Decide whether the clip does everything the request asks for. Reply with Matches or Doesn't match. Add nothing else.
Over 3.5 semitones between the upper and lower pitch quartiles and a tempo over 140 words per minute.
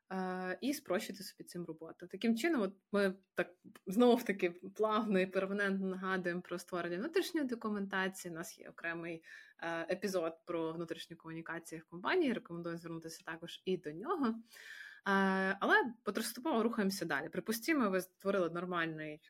Matches